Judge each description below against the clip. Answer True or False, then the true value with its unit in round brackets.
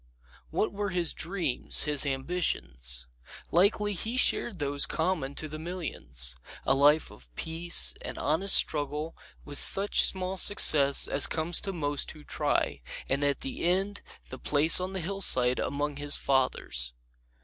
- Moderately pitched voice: True (155 Hz)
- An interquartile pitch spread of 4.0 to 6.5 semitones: True (4.8 semitones)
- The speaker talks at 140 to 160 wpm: True (150 wpm)